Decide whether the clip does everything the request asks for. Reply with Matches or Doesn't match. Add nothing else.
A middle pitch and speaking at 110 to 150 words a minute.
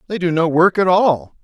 Doesn't match